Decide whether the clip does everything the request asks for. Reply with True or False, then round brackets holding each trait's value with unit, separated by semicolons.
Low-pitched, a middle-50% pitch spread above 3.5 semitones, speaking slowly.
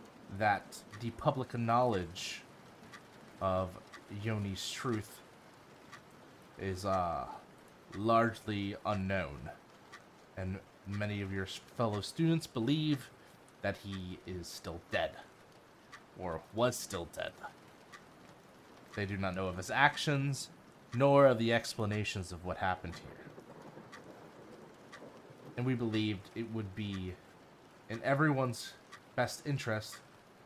True (105 Hz; 4.4 semitones; 100 wpm)